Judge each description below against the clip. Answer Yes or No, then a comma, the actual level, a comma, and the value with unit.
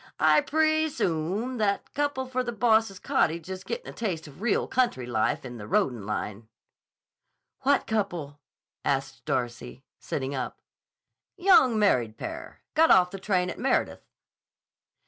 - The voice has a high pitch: Yes, high, 195 Hz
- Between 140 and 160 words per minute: Yes, average, 145 wpm